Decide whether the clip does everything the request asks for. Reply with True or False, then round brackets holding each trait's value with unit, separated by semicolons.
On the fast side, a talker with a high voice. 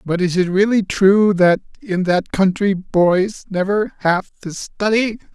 False (155 wpm; 195 Hz)